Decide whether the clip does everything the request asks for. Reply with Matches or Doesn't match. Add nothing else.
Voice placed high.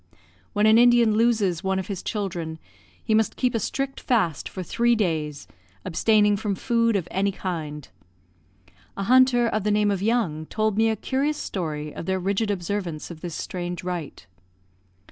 Matches